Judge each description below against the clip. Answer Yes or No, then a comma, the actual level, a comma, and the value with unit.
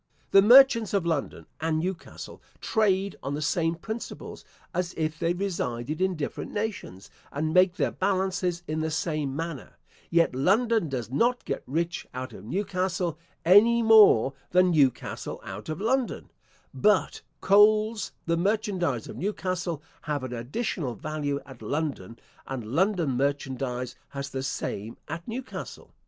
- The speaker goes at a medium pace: Yes, average, 145 wpm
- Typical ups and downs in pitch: No, wide, 5.9 semitones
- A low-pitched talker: No, medium, 170 Hz